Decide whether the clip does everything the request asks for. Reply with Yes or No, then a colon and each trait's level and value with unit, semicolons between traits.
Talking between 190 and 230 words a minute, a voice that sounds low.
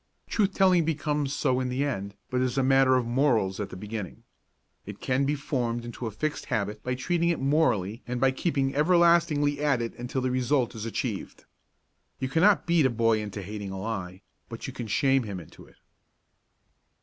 Yes: average, 195 wpm; low, 130 Hz